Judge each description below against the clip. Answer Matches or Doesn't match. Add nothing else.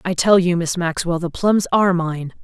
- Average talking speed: Doesn't match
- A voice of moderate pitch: Matches